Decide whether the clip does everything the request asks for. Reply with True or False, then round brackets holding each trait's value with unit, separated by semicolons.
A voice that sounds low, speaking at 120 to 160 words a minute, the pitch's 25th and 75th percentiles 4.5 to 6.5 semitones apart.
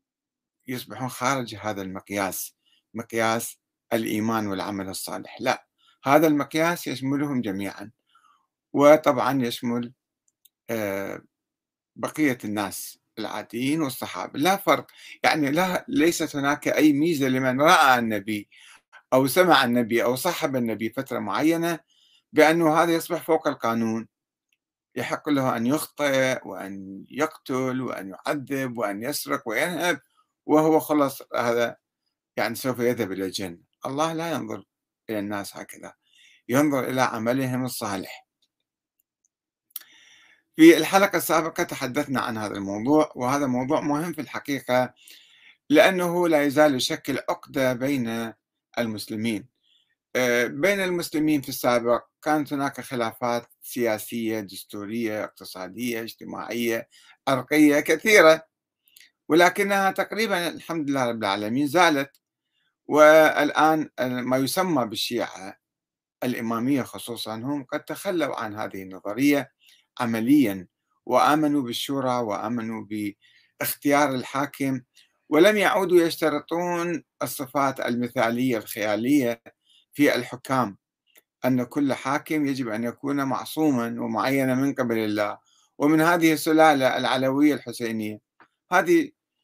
False (130 Hz; 105 wpm; 4.9 semitones)